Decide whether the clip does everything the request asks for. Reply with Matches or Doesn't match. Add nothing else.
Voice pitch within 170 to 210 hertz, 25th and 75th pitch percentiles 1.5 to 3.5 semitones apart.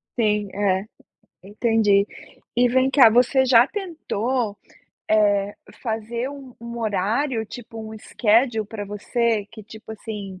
Doesn't match